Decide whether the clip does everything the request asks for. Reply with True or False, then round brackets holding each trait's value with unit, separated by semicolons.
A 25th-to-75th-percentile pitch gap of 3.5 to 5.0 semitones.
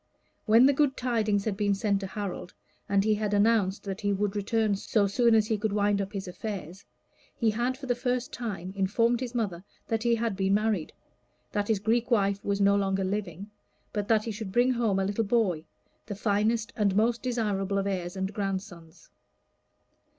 False (2.5 semitones)